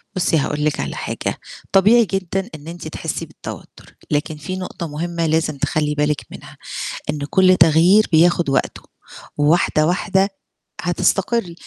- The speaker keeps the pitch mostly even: No, average, 3.4 semitones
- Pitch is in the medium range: Yes, medium, 165 Hz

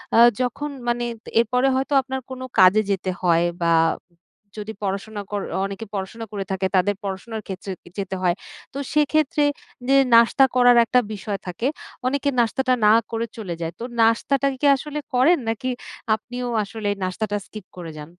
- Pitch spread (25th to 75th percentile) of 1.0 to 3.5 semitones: No, average, 4.7 semitones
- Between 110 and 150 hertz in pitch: No, high, 225 Hz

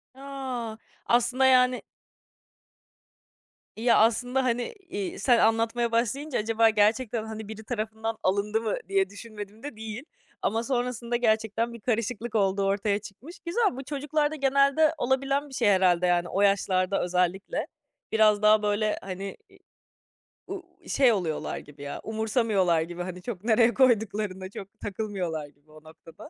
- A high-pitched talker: Yes, high, 220 Hz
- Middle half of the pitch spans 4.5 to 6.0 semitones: No, average, 3.9 semitones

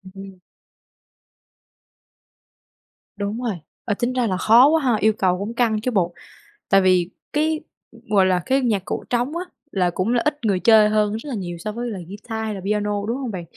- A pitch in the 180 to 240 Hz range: Yes, high, 215 Hz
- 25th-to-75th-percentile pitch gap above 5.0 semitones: No, average, 3.8 semitones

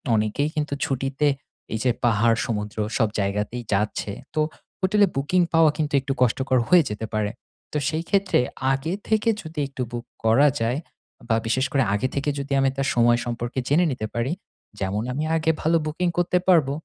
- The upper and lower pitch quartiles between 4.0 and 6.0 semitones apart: Yes, average, 5.3 semitones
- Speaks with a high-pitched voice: No, low, 135 Hz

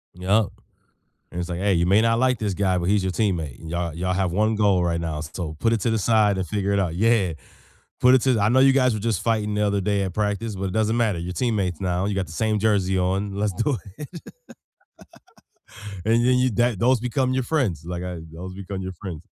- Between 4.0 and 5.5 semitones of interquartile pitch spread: No, average, 3.6 semitones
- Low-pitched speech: Yes, low, 100 Hz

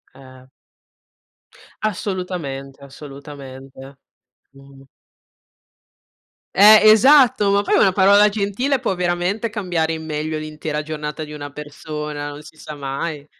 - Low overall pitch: No, medium, 155 Hz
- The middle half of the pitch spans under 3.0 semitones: No, wide, 5.6 semitones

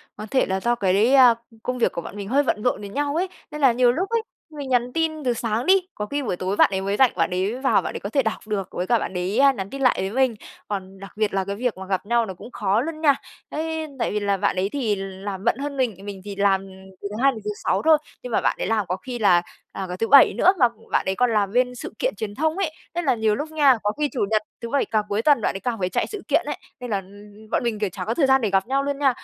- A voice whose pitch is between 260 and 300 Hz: No, high, 225 Hz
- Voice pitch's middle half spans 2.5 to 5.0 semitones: No, wide, 5.5 semitones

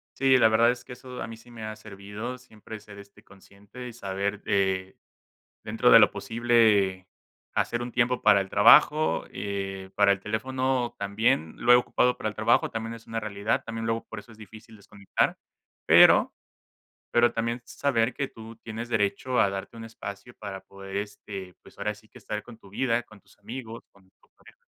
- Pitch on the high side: No, low, 110 Hz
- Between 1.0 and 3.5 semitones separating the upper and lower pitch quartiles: Yes, average, 2.9 semitones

